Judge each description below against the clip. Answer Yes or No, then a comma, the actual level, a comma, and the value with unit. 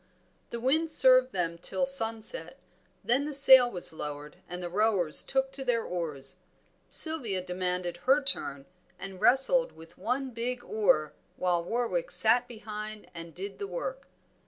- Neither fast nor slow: Yes, average, 150 wpm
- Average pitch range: No, wide, 7.0 semitones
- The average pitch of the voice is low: No, high, 225 Hz